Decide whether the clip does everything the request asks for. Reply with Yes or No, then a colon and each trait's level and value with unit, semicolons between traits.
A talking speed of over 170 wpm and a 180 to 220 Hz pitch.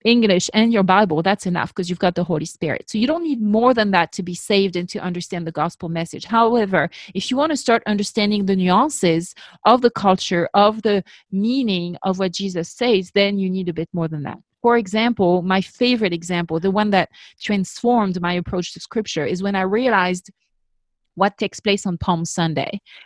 Yes: fast, 205 wpm; high, 190 Hz